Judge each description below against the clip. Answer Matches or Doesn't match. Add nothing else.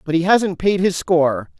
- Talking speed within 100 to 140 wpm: Doesn't match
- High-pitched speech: Doesn't match